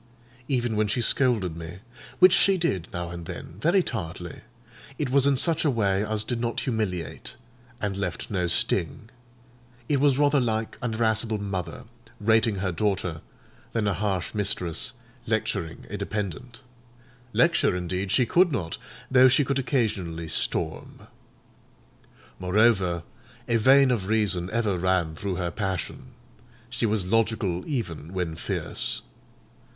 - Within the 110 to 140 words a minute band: Yes, slow, 135 wpm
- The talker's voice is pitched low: Yes, low, 105 Hz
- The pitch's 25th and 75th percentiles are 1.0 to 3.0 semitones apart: No, average, 5.1 semitones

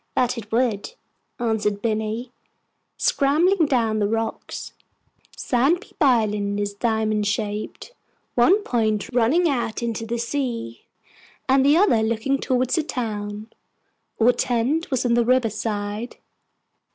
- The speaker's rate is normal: No, slow, 125 wpm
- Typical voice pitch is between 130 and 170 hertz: No, high, 230 Hz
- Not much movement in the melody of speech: No, average, 3.2 semitones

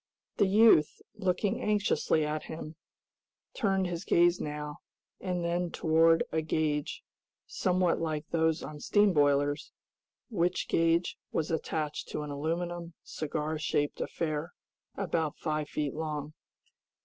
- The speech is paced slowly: Yes, slow, 125 wpm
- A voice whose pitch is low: No, medium, 160 Hz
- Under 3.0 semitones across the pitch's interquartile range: Yes, narrow, 2.5 semitones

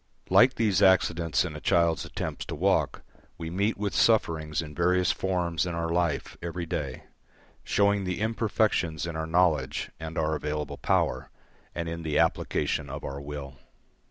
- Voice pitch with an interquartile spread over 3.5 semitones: No, average, 3.1 semitones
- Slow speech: No, average, 160 wpm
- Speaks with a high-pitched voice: No, very low, 85 Hz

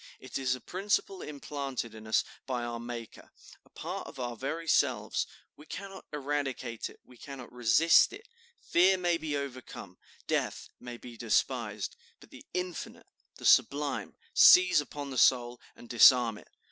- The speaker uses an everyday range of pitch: Yes, average, 4.0 semitones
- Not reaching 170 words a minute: Yes, average, 160 wpm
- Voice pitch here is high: No, low, 130 Hz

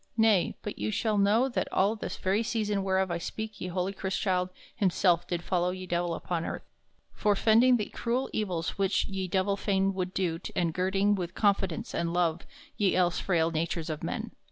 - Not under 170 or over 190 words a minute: Yes, average, 185 wpm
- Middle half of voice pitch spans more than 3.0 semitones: No, average, 2.7 semitones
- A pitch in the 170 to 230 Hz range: Yes, high, 190 Hz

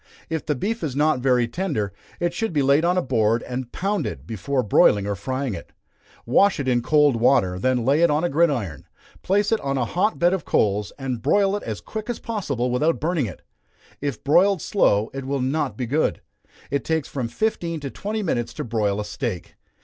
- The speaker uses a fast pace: Yes, fast, 210 wpm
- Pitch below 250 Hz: Yes, medium, 140 Hz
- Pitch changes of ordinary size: No, wide, 6.2 semitones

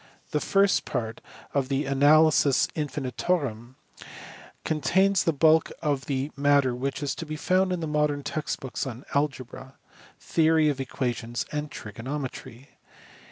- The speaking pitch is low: No, medium, 145 Hz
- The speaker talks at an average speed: No, slow, 130 wpm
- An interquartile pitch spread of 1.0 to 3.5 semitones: Yes, average, 2.8 semitones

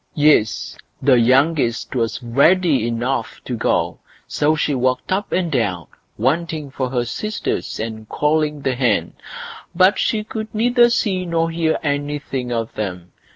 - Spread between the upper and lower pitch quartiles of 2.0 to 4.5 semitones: No, wide, 5.6 semitones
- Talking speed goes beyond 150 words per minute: No, average, 145 wpm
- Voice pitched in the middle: Yes, medium, 145 Hz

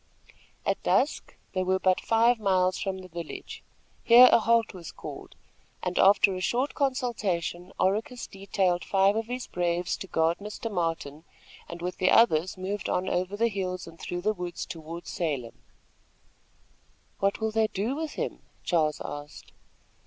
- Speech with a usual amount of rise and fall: Yes, average, 3.8 semitones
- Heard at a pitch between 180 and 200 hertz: Yes, medium, 185 Hz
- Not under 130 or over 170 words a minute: Yes, average, 160 wpm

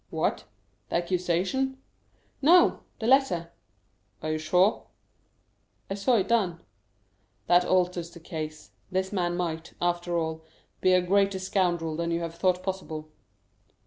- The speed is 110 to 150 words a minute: Yes, slow, 135 wpm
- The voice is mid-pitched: Yes, medium, 180 Hz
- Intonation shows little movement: Yes, narrow, 2.2 semitones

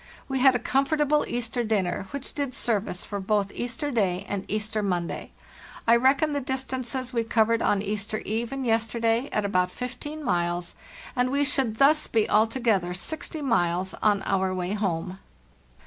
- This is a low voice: No, high, 225 Hz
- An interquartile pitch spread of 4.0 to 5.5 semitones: Yes, average, 4.9 semitones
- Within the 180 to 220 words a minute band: No, average, 165 wpm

